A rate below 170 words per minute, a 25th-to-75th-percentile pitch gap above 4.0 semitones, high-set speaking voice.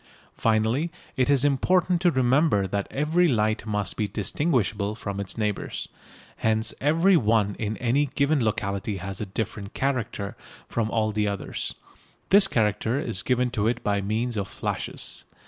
No: average, 155 wpm; average, 4.9 semitones; low, 110 Hz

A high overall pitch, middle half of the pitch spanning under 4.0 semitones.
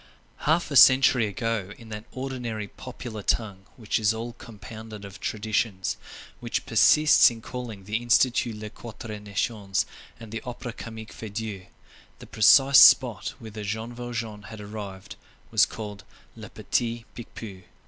No: low, 110 Hz; narrow, 2.4 semitones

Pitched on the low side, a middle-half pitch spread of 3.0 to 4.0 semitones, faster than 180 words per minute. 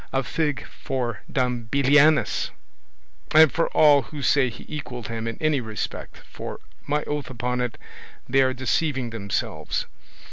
No: low, 130 Hz; average, 3.4 semitones; average, 145 wpm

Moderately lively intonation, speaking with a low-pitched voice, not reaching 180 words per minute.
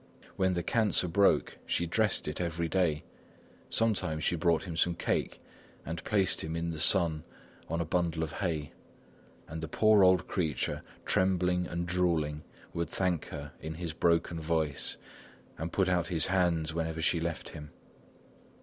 No: narrow, 2.1 semitones; very low, 85 Hz; average, 160 wpm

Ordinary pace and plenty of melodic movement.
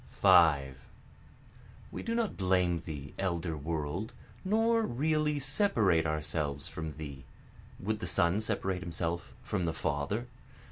No: slow, 125 wpm; wide, 6.5 semitones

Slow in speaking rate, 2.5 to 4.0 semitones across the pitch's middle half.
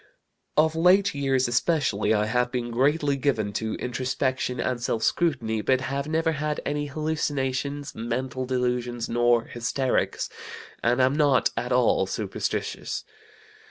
Yes: slow, 130 wpm; average, 3.3 semitones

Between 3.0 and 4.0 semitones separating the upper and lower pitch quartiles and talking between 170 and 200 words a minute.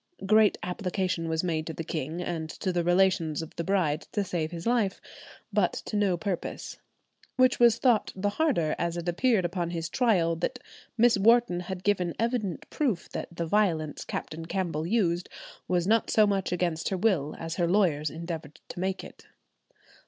Yes: average, 3.7 semitones; average, 180 wpm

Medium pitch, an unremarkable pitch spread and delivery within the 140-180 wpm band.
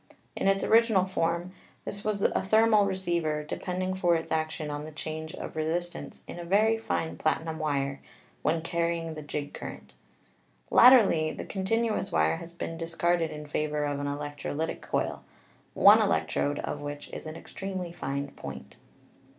Yes: medium, 165 Hz; average, 3.8 semitones; average, 165 wpm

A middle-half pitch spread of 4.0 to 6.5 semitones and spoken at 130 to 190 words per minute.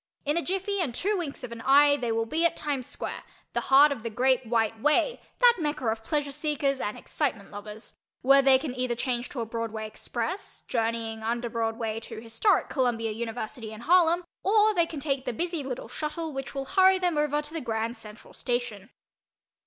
No: average, 5.1 semitones; average, 200 wpm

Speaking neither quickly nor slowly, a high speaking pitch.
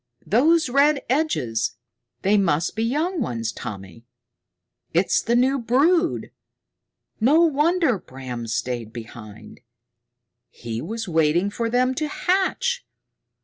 No: slow, 110 wpm; high, 230 Hz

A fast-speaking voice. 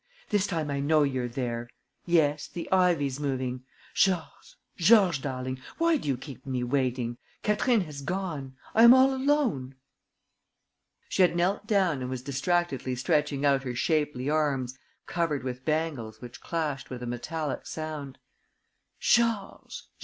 No: average, 145 wpm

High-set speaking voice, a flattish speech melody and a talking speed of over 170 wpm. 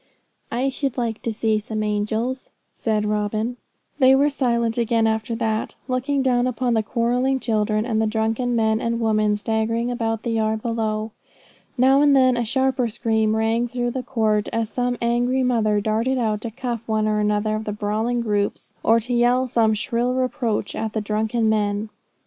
Yes: high, 225 Hz; narrow, 2.2 semitones; average, 180 wpm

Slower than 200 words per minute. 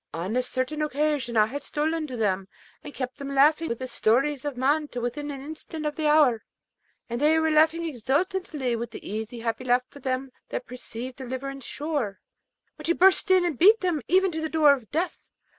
No: fast, 205 wpm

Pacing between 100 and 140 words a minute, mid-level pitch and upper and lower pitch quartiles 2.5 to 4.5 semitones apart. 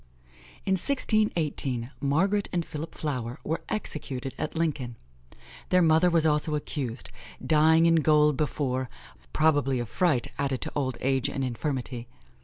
Yes: slow, 135 wpm; medium, 150 Hz; average, 3.7 semitones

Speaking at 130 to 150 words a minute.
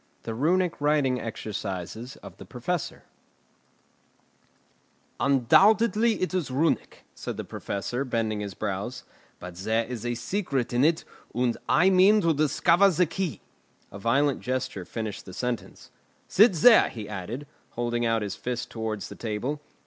Yes: average, 140 wpm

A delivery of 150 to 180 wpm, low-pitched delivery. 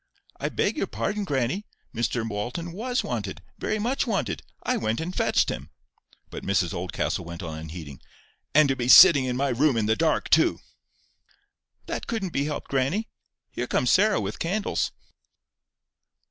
Yes: average, 160 wpm; low, 130 Hz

